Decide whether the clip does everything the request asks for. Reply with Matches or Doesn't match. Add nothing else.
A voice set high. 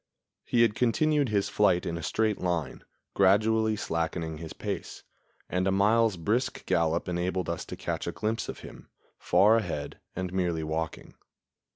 Doesn't match